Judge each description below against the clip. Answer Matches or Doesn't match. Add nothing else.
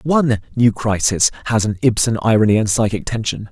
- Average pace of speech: Matches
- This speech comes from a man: Matches